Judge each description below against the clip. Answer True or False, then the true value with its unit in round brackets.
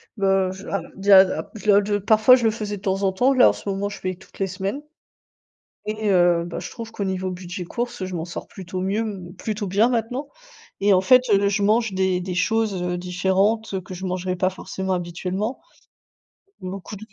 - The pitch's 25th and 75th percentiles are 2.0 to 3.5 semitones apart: True (2.6 semitones)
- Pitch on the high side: True (195 Hz)